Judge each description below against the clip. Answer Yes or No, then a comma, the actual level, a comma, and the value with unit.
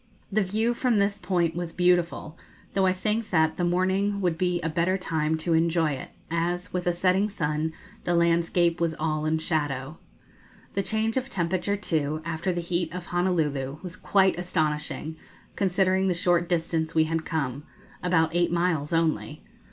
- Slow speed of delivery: No, average, 170 wpm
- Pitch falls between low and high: Yes, medium, 175 Hz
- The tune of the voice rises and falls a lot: No, narrow, 2.6 semitones